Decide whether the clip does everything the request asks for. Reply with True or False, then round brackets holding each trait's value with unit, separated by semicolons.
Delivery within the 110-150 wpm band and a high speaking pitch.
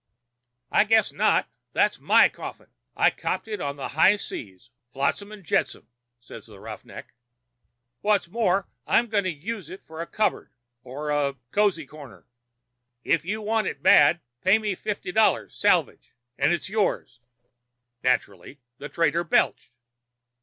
False (145 wpm; 175 Hz)